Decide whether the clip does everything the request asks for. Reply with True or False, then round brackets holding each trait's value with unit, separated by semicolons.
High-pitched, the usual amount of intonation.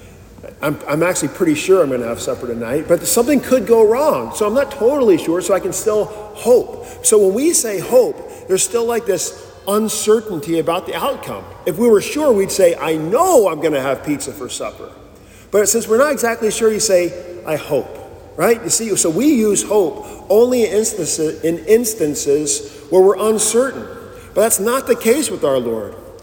False (215 Hz; 7.5 semitones)